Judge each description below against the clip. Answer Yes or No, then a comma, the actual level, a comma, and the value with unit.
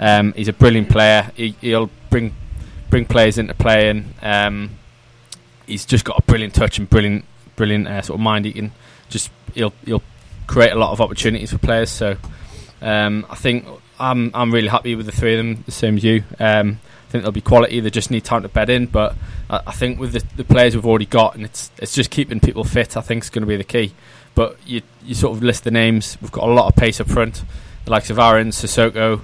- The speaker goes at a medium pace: No, fast, 240 wpm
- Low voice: Yes, low, 110 Hz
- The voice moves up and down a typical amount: No, narrow, 1.8 semitones